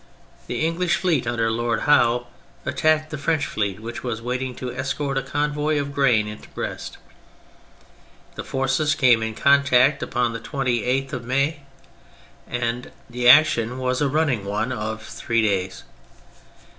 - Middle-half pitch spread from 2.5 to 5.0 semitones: Yes, average, 3.5 semitones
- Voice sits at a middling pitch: No, low, 125 Hz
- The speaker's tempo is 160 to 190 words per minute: No, average, 150 wpm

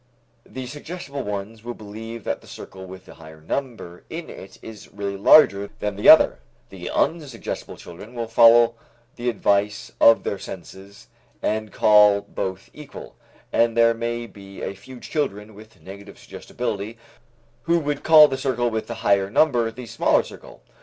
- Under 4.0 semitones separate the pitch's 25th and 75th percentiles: Yes, average, 3.3 semitones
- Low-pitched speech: Yes, low, 110 Hz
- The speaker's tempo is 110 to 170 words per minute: Yes, average, 160 wpm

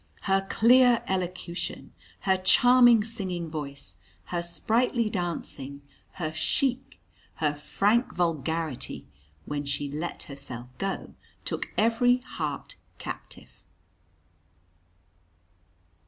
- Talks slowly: Yes, slow, 90 wpm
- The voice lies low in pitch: No, medium, 175 Hz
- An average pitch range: No, wide, 7.4 semitones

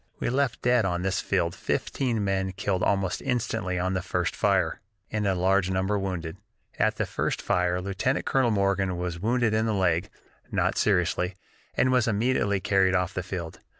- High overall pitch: No, very low, 95 Hz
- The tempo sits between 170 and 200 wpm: Yes, average, 180 wpm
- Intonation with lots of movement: No, average, 2.9 semitones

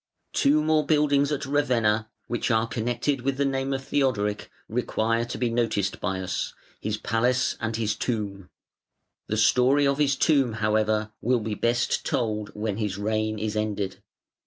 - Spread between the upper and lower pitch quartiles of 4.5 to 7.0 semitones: No, average, 3.9 semitones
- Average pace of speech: Yes, average, 160 wpm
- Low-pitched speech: Yes, low, 115 Hz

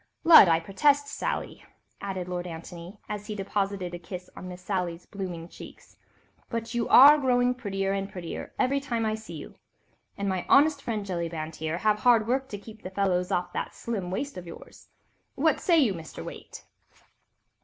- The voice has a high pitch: Yes, high, 195 Hz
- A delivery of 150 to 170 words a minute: No, average, 180 wpm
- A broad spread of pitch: No, average, 4.8 semitones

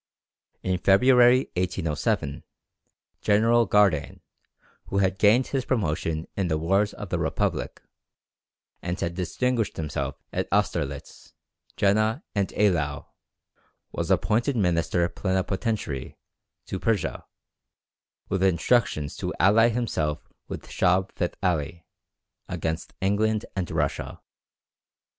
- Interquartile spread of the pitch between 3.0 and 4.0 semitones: No, average, 4.4 semitones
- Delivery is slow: Yes, slow, 105 wpm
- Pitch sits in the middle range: No, very low, 95 Hz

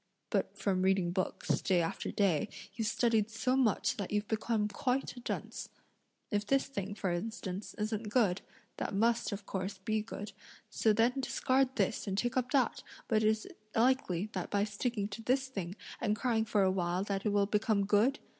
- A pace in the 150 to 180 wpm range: No, average, 190 wpm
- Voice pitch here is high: Yes, high, 210 Hz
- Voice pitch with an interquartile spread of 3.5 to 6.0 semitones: No, average, 2.9 semitones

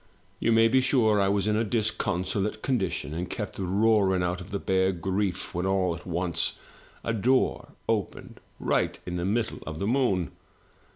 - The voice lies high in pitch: No, very low, 95 Hz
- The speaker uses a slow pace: No, average, 175 wpm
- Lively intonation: No, average, 3.5 semitones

